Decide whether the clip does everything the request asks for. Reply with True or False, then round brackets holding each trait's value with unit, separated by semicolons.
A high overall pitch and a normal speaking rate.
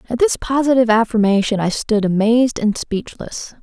True (230 Hz; 150 wpm)